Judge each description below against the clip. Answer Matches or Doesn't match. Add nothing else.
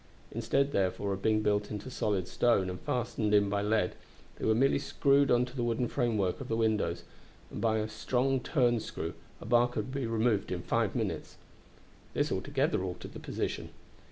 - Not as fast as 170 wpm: Doesn't match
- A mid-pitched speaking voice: Doesn't match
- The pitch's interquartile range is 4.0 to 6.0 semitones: Doesn't match